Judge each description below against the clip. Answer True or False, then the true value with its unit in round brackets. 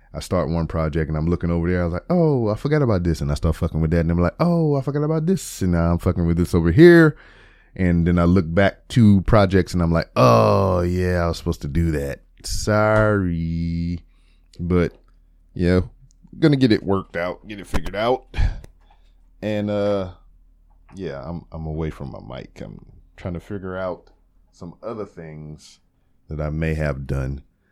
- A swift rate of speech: False (195 wpm)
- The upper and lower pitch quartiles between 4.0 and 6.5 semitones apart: False (3.3 semitones)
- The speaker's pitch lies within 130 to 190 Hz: False (85 Hz)